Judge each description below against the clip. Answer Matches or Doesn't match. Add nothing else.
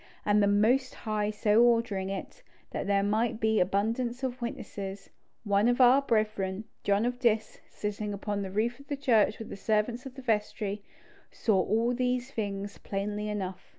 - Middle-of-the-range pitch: Doesn't match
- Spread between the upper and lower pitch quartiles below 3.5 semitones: Matches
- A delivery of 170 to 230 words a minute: Matches